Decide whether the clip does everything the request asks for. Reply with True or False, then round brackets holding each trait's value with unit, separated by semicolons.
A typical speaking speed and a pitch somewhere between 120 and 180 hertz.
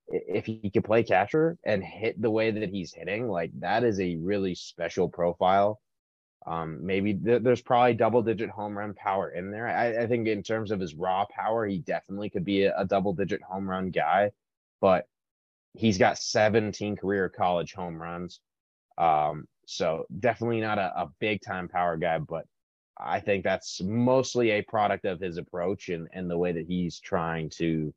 False (185 wpm; 100 Hz)